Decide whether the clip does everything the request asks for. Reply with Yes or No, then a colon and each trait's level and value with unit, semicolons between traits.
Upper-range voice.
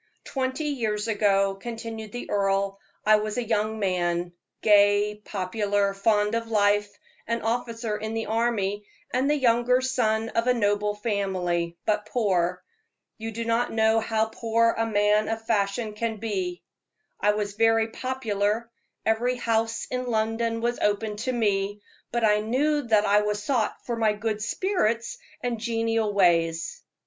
Yes: high, 220 Hz